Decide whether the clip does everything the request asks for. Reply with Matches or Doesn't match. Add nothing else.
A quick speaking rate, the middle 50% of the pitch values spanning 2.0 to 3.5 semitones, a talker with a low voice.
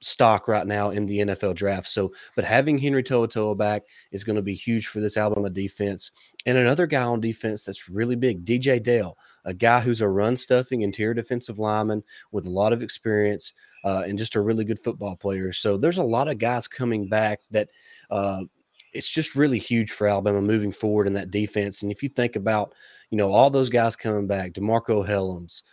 Matches